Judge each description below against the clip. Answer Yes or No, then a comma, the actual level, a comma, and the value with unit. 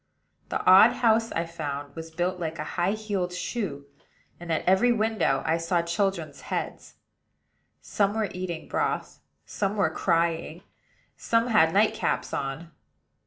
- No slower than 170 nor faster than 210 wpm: No, average, 145 wpm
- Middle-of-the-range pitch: Yes, medium, 175 Hz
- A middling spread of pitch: Yes, average, 4.3 semitones